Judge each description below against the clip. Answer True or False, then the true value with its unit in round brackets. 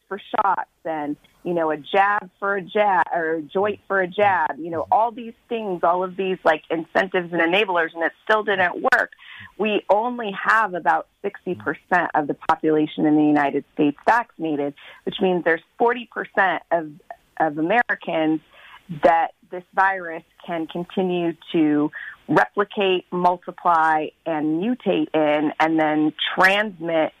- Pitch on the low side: False (175 Hz)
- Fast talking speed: False (150 wpm)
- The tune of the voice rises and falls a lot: False (4.0 semitones)